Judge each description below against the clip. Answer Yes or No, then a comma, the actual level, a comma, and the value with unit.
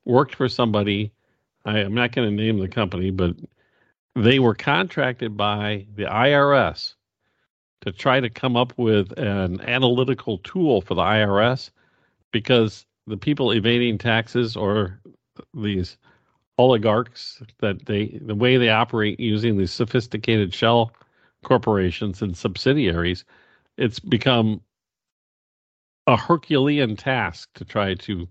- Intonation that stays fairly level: No, average, 3.3 semitones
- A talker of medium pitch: No, low, 110 Hz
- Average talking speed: No, slow, 125 wpm